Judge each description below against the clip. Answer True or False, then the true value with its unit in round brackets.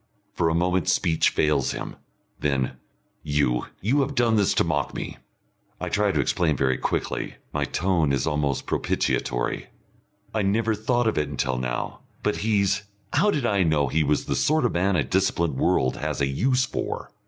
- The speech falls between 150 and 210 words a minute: True (180 wpm)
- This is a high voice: False (85 Hz)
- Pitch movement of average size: False (6.8 semitones)